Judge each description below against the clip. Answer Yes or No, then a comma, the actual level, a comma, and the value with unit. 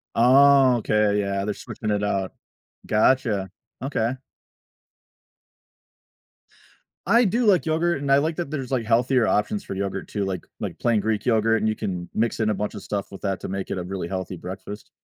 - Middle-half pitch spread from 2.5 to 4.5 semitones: No, average, 5.2 semitones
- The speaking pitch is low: Yes, low, 110 Hz